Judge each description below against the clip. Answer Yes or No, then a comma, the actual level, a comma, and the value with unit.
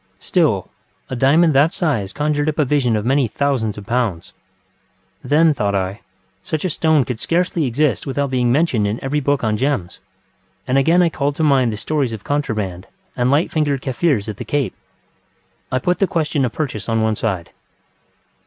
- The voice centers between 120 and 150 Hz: Yes, low, 135 Hz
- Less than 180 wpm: No, average, 185 wpm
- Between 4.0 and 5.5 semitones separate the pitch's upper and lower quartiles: Yes, average, 5.1 semitones